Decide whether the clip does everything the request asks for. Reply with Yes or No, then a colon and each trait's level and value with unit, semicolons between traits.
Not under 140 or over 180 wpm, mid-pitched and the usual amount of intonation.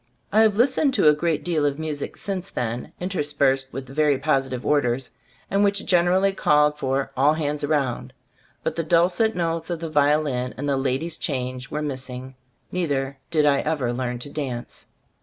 Yes: average, 175 wpm; medium, 150 Hz; average, 3.9 semitones